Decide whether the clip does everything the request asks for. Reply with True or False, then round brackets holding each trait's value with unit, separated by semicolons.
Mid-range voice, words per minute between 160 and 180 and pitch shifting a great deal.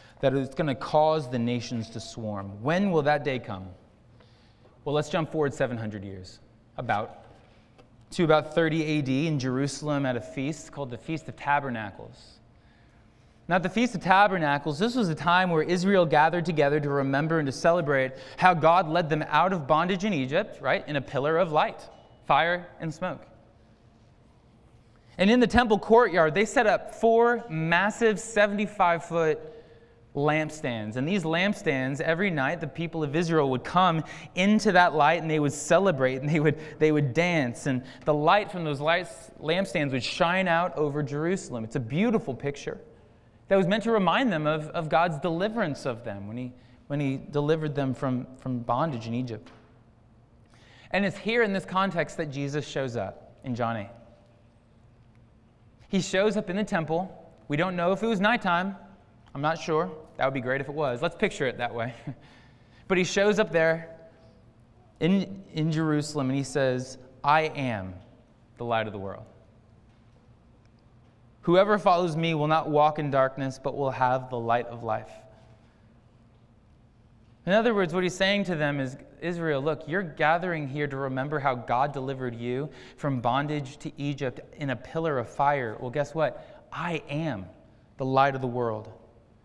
True (145 Hz; 175 wpm; 6.0 semitones)